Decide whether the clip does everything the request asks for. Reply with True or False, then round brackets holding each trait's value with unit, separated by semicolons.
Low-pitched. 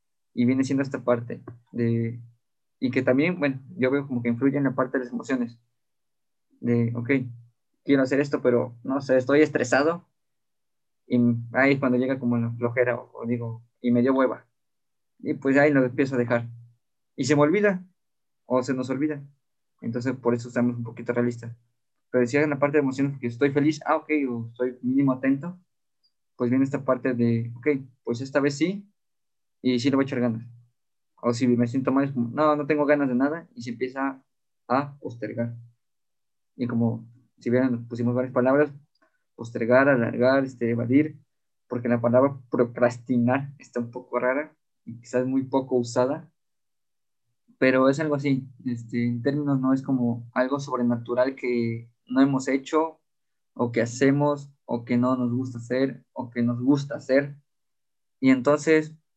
True (130 Hz)